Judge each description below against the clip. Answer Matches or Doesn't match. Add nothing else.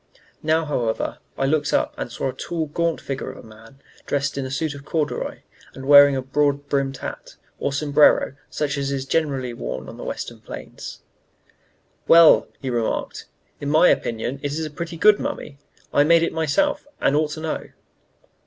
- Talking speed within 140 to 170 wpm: Doesn't match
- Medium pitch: Matches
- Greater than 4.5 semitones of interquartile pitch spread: Doesn't match